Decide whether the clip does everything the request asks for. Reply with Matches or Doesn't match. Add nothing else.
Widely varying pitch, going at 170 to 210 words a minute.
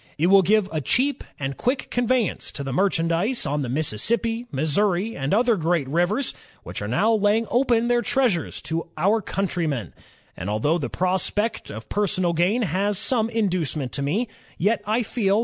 Matches